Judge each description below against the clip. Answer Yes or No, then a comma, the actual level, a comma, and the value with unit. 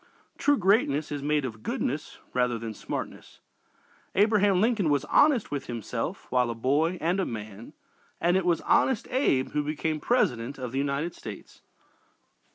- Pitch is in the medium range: Yes, medium, 150 Hz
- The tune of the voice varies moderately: No, wide, 7.3 semitones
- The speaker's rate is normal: Yes, average, 160 wpm